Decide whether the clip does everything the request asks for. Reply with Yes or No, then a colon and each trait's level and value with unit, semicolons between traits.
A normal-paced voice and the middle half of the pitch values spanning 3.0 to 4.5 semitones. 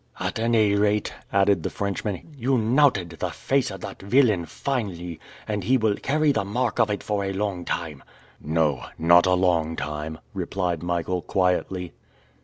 Yes: average, 165 wpm; average, 4.1 semitones